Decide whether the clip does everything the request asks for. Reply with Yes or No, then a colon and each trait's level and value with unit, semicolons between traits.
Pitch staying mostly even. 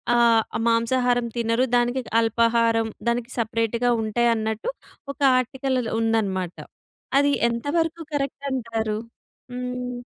Yes: narrow, 1.8 semitones